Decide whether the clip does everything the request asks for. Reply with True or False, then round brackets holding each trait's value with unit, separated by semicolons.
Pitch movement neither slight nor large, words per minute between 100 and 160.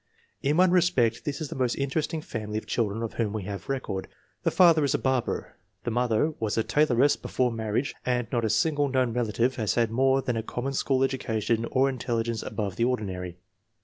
False (3.4 semitones; 205 wpm)